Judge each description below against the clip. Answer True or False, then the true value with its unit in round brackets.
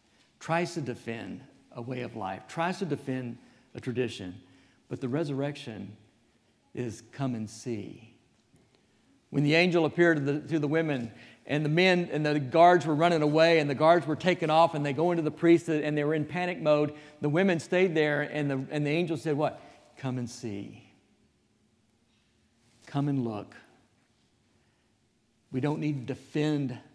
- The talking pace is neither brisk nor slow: True (170 wpm)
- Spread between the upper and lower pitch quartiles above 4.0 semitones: True (5.2 semitones)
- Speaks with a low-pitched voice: False (145 Hz)